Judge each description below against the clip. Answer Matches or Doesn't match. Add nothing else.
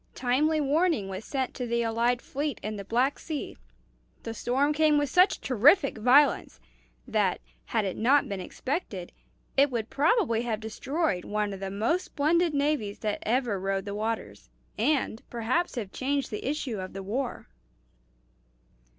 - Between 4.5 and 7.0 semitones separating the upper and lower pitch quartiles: Matches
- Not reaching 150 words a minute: Doesn't match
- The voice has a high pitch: Matches